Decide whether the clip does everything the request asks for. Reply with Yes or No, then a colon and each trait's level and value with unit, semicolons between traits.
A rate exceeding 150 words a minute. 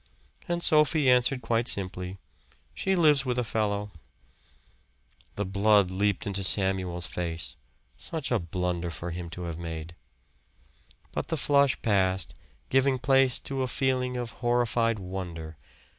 No: average, 140 wpm